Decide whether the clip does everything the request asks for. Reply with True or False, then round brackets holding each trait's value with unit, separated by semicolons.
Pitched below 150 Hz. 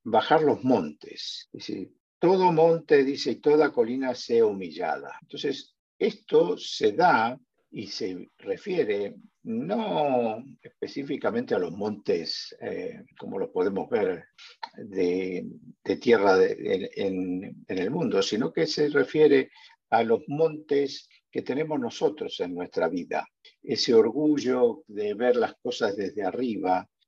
False (165 Hz)